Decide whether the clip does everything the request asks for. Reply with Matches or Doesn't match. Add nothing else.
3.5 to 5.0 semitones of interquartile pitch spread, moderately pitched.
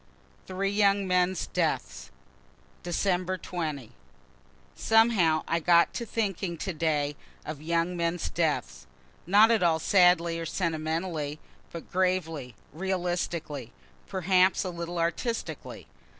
Doesn't match